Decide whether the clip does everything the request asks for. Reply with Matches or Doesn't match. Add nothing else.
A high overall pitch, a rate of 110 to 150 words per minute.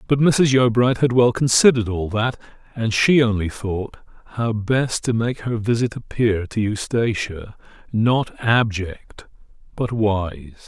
Doesn't match